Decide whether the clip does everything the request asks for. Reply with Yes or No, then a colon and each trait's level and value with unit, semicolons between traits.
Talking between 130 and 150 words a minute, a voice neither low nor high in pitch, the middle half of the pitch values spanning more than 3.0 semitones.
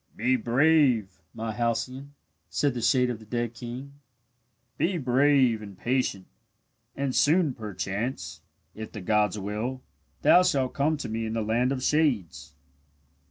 No: average, 145 wpm; low, 120 Hz; average, 4.0 semitones